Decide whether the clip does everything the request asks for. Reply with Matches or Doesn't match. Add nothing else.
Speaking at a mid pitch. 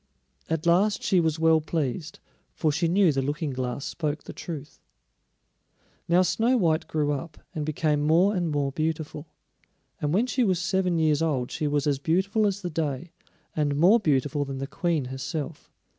Matches